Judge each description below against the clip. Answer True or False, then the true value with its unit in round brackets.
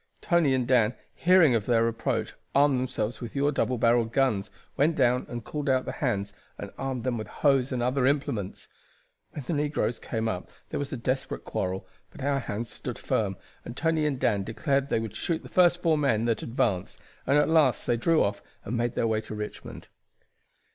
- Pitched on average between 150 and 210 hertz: False (125 Hz)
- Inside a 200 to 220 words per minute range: True (205 wpm)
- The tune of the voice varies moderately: True (4.0 semitones)